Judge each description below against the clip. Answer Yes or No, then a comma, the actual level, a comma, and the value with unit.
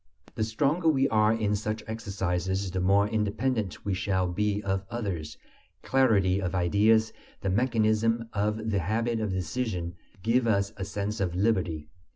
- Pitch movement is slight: No, average, 3.0 semitones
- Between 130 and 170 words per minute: Yes, average, 155 wpm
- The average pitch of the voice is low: Yes, low, 105 Hz